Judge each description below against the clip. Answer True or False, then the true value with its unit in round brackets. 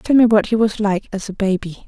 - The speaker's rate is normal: False (290 wpm)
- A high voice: True (205 Hz)